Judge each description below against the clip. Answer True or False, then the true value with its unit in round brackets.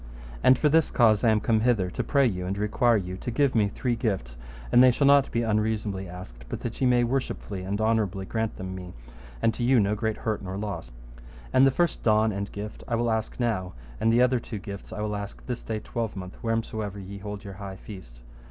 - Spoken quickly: True (230 wpm)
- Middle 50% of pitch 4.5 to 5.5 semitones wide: False (3.2 semitones)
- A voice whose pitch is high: False (110 Hz)